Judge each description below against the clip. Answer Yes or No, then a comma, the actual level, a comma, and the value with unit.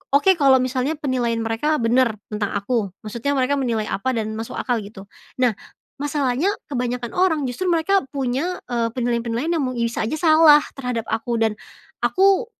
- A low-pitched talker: No, very high, 250 Hz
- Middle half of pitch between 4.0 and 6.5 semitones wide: Yes, average, 4.4 semitones